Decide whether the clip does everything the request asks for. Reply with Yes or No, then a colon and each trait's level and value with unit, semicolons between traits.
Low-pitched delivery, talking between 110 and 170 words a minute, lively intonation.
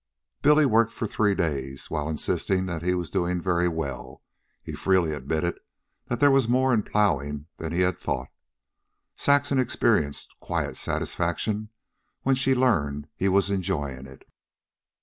Yes: very low, 90 Hz; average, 150 wpm; wide, 6.7 semitones